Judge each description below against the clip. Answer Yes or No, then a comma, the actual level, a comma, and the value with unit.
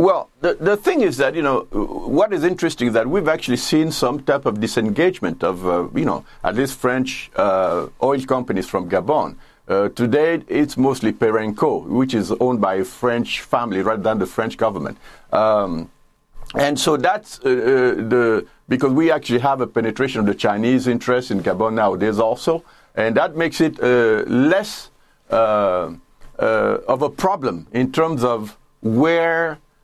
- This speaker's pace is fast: No, average, 170 wpm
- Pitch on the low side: Yes, low, 125 Hz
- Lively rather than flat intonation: Yes, wide, 5.9 semitones